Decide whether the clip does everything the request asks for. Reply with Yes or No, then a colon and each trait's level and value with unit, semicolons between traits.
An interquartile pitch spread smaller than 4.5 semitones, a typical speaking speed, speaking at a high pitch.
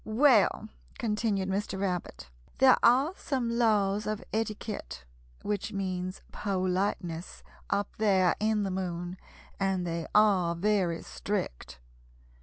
No: average, 3.0 semitones; slow, 110 wpm; high, 195 Hz